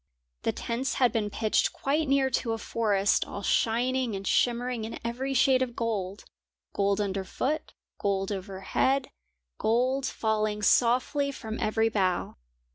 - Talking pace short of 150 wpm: Yes, average, 140 wpm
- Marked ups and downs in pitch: No, average, 3.9 semitones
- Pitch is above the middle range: Yes, high, 230 Hz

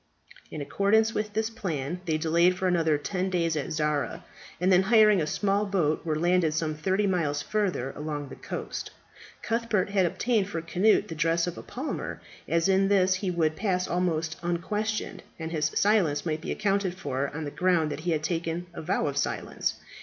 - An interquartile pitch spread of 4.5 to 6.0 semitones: No, average, 3.8 semitones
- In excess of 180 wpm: Yes, average, 190 wpm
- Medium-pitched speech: Yes, medium, 175 Hz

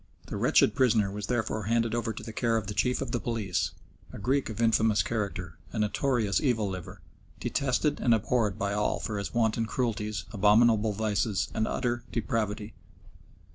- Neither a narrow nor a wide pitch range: No, narrow, 2.3 semitones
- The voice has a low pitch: Yes, low, 110 Hz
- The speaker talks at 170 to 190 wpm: Yes, average, 175 wpm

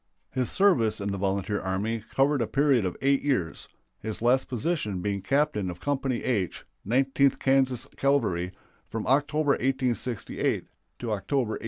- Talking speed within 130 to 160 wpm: Yes, average, 150 wpm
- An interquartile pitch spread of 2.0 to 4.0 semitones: No, average, 5.0 semitones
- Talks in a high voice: No, low, 125 Hz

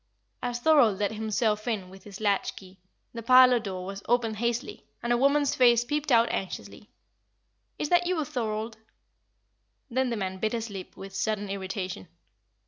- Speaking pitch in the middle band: No, high, 220 Hz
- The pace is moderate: Yes, average, 165 wpm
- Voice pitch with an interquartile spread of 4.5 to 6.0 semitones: No, average, 3.8 semitones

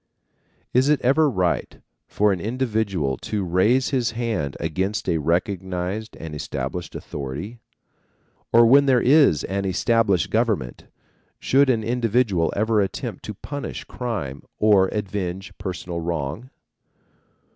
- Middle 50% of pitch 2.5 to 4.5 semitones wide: No, average, 5.0 semitones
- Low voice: Yes, low, 105 Hz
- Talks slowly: Yes, slow, 125 wpm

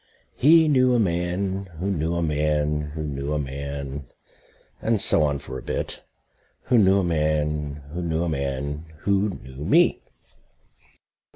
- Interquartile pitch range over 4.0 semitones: Yes, average, 4.8 semitones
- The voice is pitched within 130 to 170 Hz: No, very low, 75 Hz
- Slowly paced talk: No, average, 155 wpm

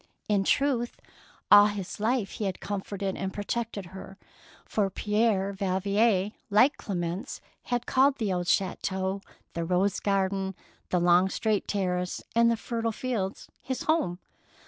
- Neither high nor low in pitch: No, high, 200 Hz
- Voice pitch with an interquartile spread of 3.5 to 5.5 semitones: No, average, 3.0 semitones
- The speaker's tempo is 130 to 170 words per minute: Yes, average, 140 wpm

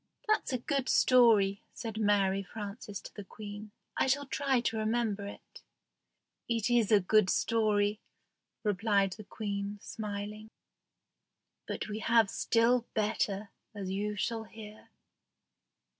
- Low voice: No, high, 215 Hz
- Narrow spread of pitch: Yes, narrow, 2.1 semitones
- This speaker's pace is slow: Yes, slow, 130 wpm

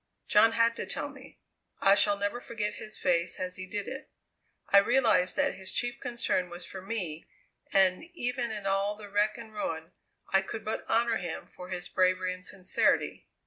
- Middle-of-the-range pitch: No, high, 200 Hz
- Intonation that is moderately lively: Yes, average, 3.6 semitones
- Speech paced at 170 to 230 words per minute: Yes, average, 185 wpm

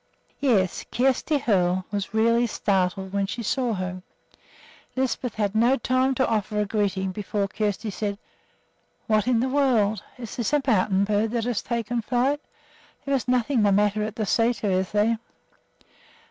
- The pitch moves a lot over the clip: No, average, 3.4 semitones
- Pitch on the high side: Yes, high, 220 Hz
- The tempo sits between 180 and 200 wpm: No, average, 160 wpm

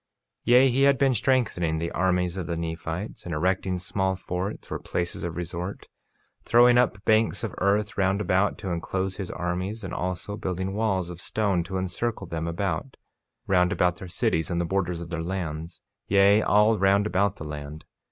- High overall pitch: No, very low, 95 Hz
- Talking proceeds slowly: No, average, 185 wpm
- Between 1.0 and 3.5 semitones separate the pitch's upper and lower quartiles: Yes, average, 2.9 semitones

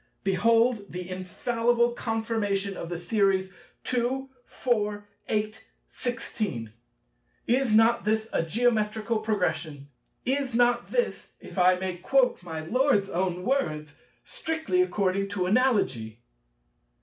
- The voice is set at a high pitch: Yes, high, 215 Hz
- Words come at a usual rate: No, slow, 105 wpm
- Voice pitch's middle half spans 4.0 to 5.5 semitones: Yes, average, 4.7 semitones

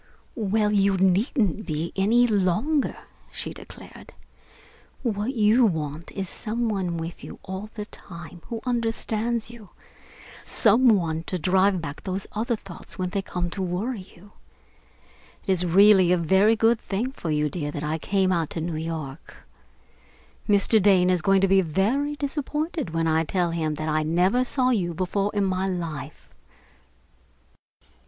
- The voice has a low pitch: No, high, 190 Hz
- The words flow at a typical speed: Yes, average, 160 wpm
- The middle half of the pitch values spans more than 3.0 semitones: Yes, average, 4.3 semitones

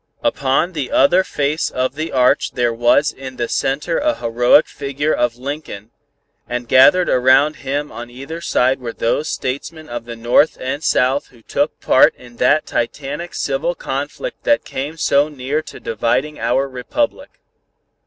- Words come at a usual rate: Yes, average, 160 wpm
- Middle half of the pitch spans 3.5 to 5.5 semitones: Yes, average, 3.9 semitones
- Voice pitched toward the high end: No, low, 135 Hz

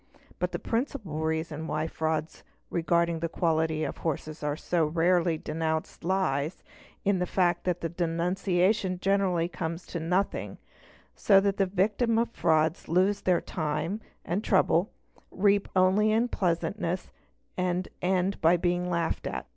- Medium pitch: Yes, medium, 175 Hz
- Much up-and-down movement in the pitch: No, average, 2.9 semitones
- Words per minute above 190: No, average, 145 wpm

